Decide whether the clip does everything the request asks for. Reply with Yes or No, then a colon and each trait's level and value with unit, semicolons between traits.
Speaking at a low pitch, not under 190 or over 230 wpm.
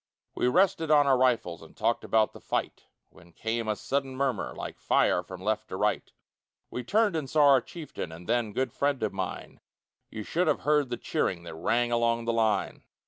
Yes: low, 120 Hz; average, 200 wpm